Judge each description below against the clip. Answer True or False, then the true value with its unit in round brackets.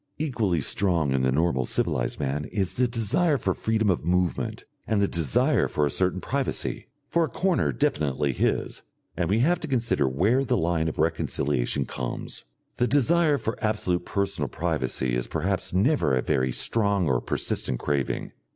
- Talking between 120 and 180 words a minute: True (170 wpm)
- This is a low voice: True (90 Hz)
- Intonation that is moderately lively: False (8.1 semitones)